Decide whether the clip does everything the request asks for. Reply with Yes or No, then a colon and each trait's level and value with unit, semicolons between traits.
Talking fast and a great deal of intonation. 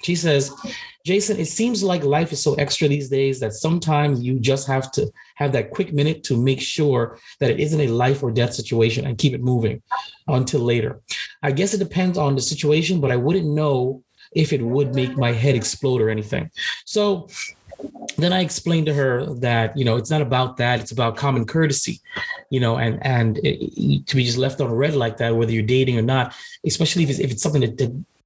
No: fast, 220 wpm; average, 3.8 semitones